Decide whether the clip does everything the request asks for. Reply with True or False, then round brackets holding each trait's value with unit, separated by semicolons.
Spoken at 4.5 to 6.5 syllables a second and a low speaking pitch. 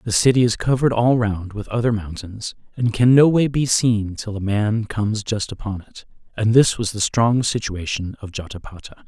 True (5.0 syllables/s; 110 Hz)